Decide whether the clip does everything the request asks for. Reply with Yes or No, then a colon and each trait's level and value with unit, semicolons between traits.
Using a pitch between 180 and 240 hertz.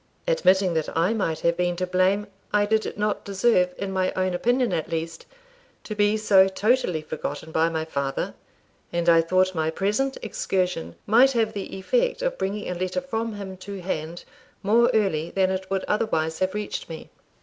Yes: high, 190 Hz